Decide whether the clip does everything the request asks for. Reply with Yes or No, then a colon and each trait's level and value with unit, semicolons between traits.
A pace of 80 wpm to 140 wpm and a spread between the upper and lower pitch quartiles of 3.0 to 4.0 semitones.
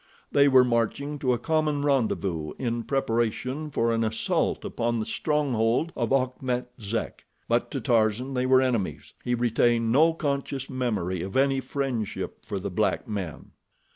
No: average, 150 wpm; average, 3.3 semitones